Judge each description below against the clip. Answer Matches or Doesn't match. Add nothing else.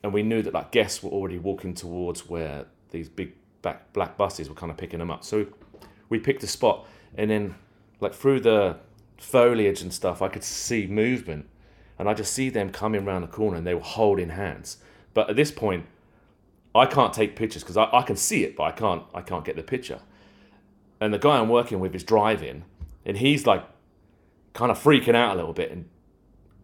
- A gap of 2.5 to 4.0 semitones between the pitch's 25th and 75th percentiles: Matches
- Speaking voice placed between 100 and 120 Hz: Matches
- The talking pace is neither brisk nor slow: Doesn't match